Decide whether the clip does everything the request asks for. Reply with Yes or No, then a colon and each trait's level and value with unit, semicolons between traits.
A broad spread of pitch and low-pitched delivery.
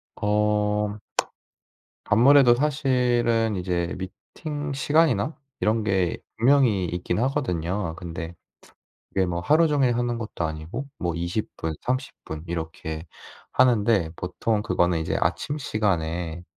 Yes: wide, 6.3 semitones; low, 105 Hz